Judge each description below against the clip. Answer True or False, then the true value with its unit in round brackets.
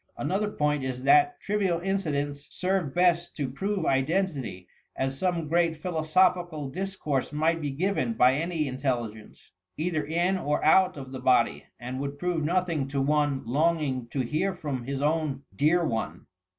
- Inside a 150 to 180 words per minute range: True (155 wpm)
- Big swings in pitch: False (4.8 semitones)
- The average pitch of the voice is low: False (155 Hz)